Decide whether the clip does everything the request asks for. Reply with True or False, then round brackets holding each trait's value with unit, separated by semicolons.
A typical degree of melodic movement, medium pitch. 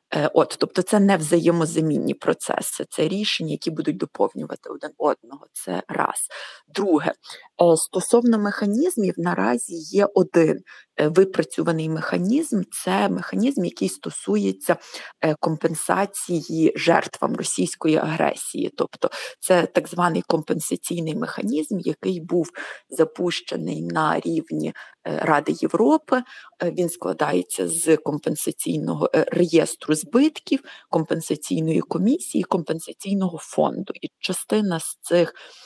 True (4.0 semitones; 175 Hz)